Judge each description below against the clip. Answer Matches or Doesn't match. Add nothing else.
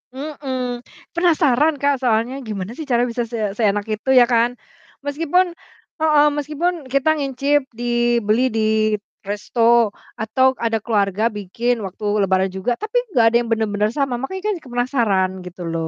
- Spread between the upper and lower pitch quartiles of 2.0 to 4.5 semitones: Doesn't match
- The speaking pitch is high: Matches